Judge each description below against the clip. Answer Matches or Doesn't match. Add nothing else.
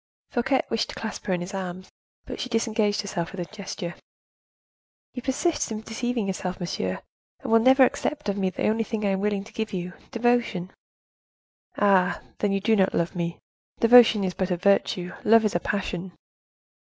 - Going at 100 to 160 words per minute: Doesn't match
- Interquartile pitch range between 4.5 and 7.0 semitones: Doesn't match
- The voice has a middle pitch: Doesn't match